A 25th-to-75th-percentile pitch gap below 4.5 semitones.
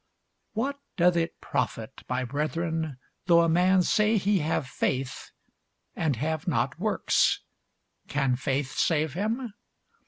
No: average, 5.2 semitones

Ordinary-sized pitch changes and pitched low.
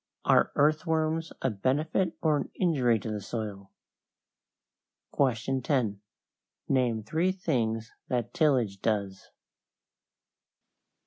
No: wide, 6.0 semitones; low, 125 Hz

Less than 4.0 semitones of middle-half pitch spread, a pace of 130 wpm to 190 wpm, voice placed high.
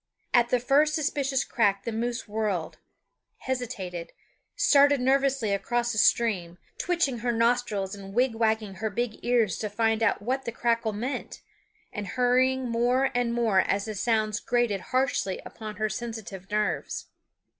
Yes: average, 3.0 semitones; average, 145 wpm; high, 230 Hz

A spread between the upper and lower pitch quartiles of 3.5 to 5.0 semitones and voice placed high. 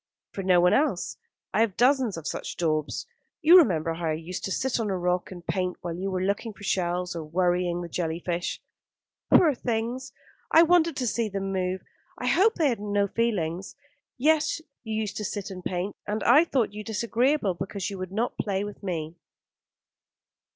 Yes: average, 4.7 semitones; high, 195 Hz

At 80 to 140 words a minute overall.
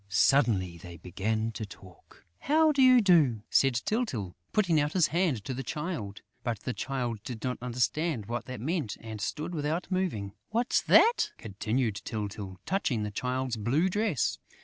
No: average, 165 wpm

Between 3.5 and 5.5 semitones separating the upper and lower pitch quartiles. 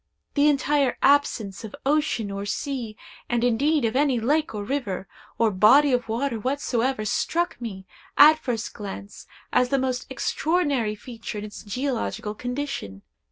Yes: average, 4.8 semitones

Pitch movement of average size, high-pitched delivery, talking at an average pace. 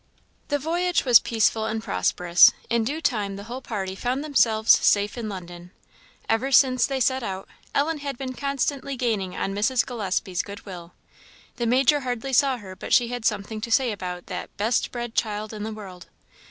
Yes: average, 4.4 semitones; high, 230 Hz; average, 185 wpm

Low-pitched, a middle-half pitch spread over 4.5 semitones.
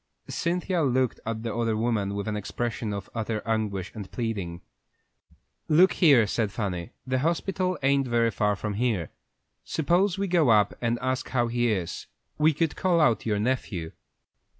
Yes: low, 115 Hz; average, 5.1 semitones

